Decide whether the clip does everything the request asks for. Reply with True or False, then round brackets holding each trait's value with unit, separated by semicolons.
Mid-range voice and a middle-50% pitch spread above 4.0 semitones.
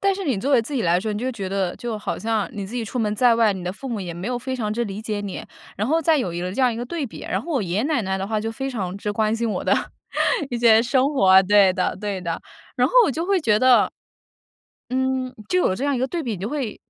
False (225 Hz; 4.5 semitones)